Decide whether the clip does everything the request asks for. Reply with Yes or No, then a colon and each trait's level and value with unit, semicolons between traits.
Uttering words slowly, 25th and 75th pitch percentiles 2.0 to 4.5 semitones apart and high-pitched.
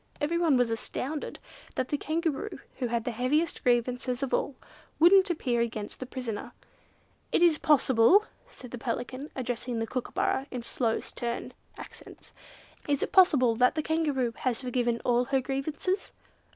No: average, 150 wpm; average, 4.1 semitones; very high, 255 Hz